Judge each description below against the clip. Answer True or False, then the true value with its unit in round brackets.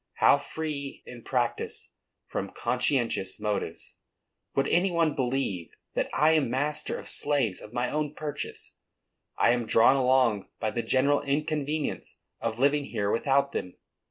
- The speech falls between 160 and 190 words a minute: False (145 wpm)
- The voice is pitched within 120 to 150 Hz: True (135 Hz)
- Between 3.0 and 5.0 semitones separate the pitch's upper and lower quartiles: True (3.9 semitones)